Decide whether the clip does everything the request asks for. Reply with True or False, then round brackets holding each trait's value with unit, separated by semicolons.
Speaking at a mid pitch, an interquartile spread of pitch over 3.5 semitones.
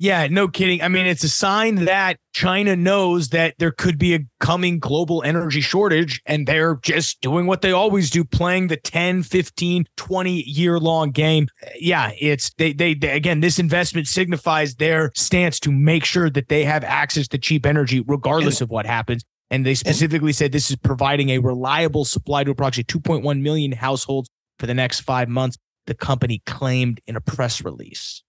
True (155 Hz; 4.3 semitones)